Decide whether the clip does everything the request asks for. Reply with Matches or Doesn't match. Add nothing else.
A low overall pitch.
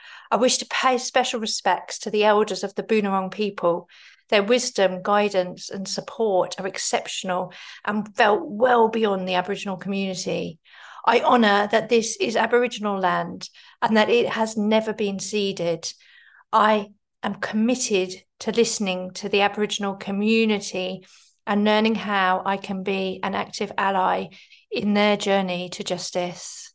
Doesn't match